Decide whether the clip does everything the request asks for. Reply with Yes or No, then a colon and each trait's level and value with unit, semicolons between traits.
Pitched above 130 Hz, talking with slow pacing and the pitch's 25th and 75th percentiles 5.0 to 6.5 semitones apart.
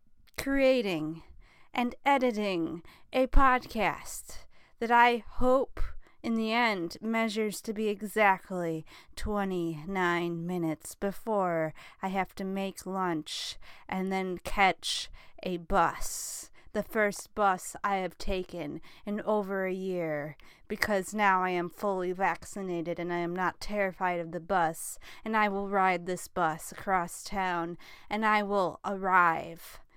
No: high, 190 Hz; slow, 130 wpm; average, 3.4 semitones